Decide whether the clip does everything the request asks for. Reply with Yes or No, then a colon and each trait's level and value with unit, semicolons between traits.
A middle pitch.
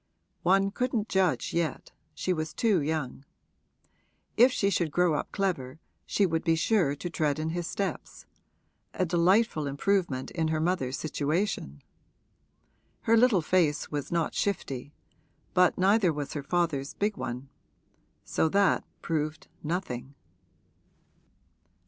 Yes: medium, 165 Hz